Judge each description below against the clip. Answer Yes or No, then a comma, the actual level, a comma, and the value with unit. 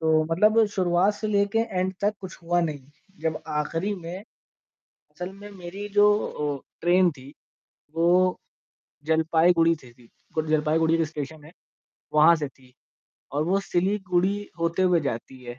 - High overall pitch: No, medium, 170 Hz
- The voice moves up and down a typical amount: Yes, average, 3.4 semitones